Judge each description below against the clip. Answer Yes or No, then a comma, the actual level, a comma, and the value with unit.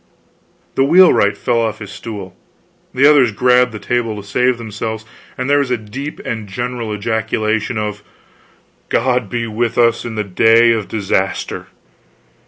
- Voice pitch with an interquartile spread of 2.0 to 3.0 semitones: Yes, average, 2.7 semitones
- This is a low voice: Yes, low, 115 Hz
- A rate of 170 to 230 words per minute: No, average, 155 wpm